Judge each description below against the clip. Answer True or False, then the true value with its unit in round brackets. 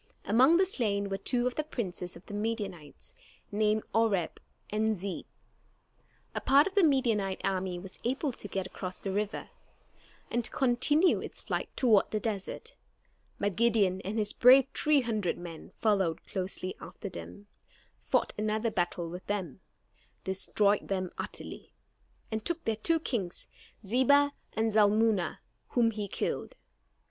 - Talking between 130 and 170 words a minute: True (150 wpm)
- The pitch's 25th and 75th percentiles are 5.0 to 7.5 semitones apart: False (4.1 semitones)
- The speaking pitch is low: False (210 Hz)